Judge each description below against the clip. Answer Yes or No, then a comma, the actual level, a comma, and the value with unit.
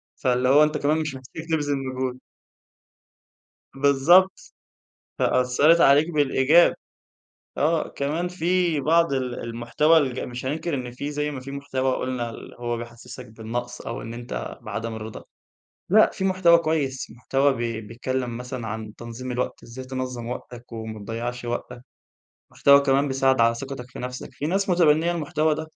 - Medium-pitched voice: No, low, 130 Hz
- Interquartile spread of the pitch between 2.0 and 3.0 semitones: No, average, 3.9 semitones